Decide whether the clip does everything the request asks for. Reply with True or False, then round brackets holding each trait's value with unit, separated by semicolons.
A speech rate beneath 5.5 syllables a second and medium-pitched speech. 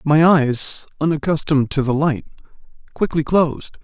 True (4.9 syllables/s; 150 Hz)